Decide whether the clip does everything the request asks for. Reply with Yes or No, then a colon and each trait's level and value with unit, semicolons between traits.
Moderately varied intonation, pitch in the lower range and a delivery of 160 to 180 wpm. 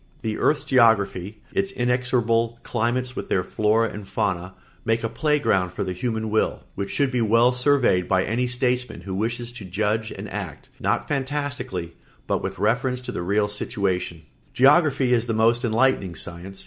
Yes: average, 4.0 semitones; low, 115 Hz; average, 175 wpm